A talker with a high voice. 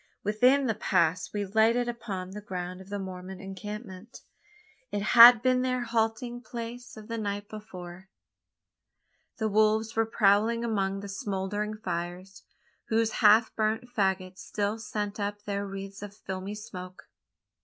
Yes: high, 210 Hz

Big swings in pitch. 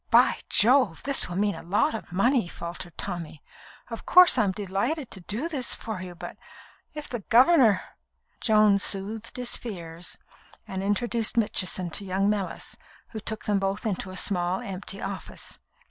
No: average, 3.8 semitones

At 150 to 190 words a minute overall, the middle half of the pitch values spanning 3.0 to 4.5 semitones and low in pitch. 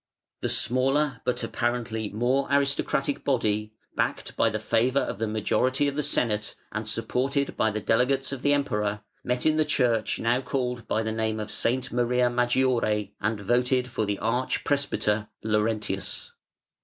Yes: average, 160 wpm; average, 3.3 semitones; low, 120 Hz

